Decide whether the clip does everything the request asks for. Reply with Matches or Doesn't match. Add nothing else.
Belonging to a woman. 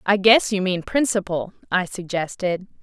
Matches